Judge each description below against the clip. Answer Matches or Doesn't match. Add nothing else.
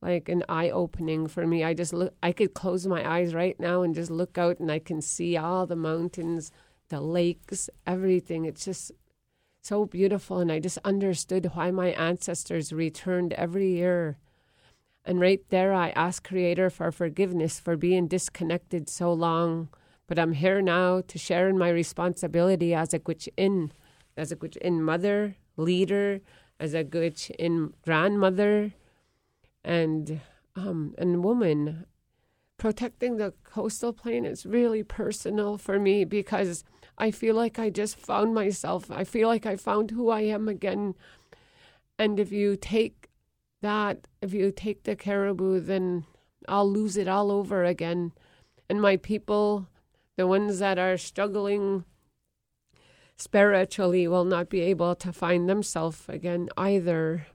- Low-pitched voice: Doesn't match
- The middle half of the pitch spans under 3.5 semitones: Matches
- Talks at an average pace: Matches